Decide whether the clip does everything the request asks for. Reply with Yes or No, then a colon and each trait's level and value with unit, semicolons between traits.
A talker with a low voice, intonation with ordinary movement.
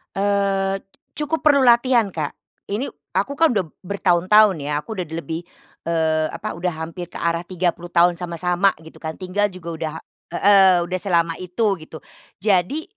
No: medium, 185 Hz; average, 3.3 semitones